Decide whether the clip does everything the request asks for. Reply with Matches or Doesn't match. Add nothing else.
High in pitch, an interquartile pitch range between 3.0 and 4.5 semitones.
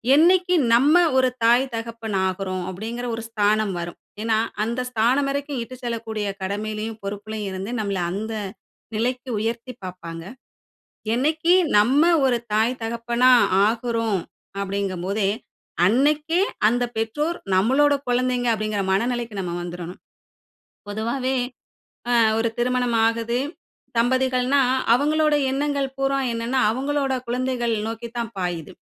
Matches